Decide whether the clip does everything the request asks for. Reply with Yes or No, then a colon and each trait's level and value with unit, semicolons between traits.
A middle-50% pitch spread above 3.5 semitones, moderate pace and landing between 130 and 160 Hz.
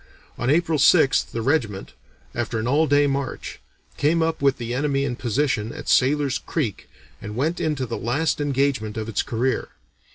Yes: average, 3.9 semitones; average, 170 wpm; low, 135 Hz